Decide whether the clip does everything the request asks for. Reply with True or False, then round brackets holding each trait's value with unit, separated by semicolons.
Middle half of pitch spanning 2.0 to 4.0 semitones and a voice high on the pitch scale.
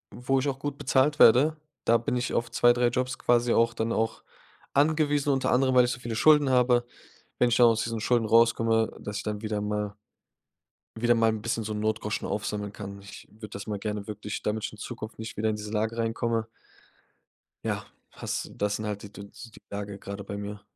False (2.6 semitones; 115 Hz)